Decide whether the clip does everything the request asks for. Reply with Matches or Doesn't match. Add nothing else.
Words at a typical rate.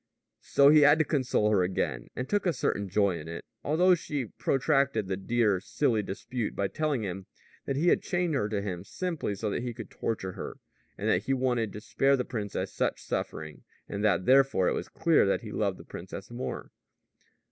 Doesn't match